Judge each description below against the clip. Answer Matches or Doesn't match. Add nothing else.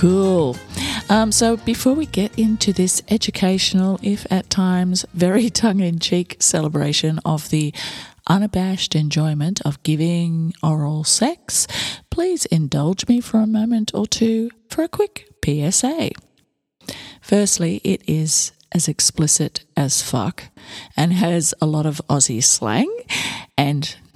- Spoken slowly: Matches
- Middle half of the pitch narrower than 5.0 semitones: Doesn't match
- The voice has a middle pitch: Matches